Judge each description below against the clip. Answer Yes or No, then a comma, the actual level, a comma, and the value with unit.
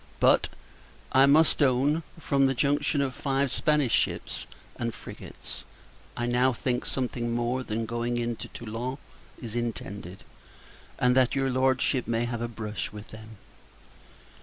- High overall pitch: No, low, 125 Hz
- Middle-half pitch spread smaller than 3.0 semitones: Yes, narrow, 2.4 semitones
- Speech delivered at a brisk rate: No, average, 140 wpm